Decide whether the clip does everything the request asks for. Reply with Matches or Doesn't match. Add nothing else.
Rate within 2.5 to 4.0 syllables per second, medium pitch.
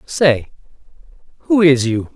Matches